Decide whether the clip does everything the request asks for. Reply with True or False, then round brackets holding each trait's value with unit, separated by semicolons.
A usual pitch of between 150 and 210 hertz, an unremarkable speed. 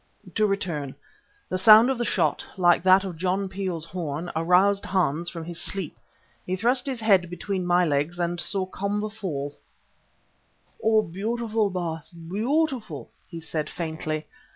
True (185 Hz; 150 wpm)